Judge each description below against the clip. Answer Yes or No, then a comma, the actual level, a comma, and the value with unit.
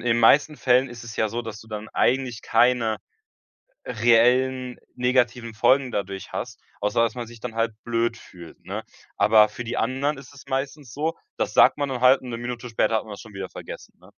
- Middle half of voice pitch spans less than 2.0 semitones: No, narrow, 2.4 semitones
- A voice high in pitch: No, low, 120 Hz